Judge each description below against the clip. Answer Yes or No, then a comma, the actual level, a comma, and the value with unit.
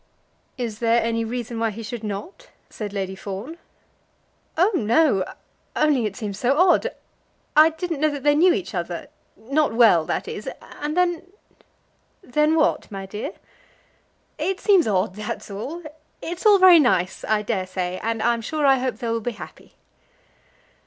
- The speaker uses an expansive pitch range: Yes, wide, 6.6 semitones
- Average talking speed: Yes, average, 165 wpm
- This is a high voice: Yes, high, 240 Hz